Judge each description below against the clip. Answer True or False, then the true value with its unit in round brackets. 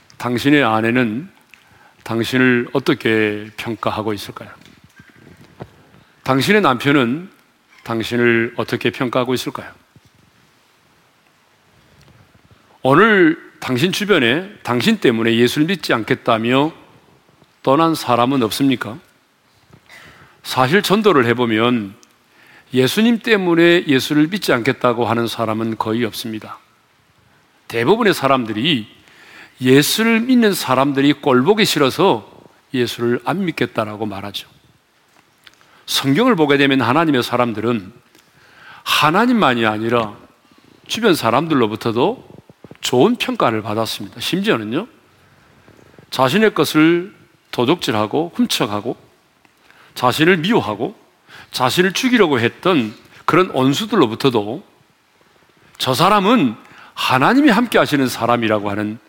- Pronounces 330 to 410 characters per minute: False (250 characters per minute)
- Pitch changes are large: True (6.1 semitones)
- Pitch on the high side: False (130 Hz)